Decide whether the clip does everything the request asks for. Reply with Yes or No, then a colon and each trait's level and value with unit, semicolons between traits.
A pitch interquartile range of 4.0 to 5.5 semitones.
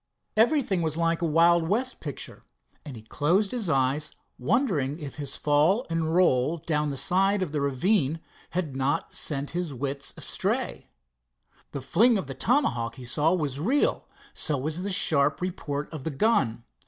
Yes: average, 4.9 semitones